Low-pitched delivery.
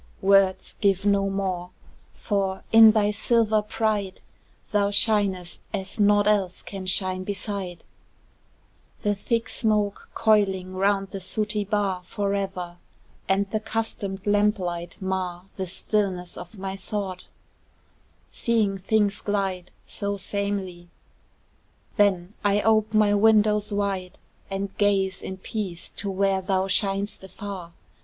No: high, 200 Hz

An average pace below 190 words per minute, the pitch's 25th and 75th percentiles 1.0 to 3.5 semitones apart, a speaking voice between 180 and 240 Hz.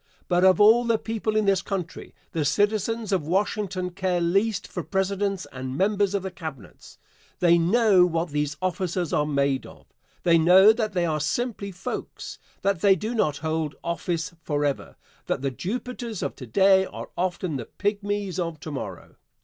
No: average, 175 wpm; average, 4.2 semitones; medium, 185 Hz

